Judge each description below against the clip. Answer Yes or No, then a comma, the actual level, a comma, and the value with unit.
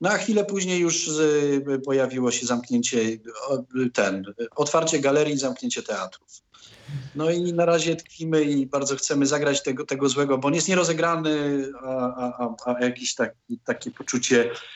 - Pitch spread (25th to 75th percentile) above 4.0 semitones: Yes, average, 4.4 semitones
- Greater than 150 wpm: No, average, 145 wpm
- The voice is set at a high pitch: No, medium, 140 Hz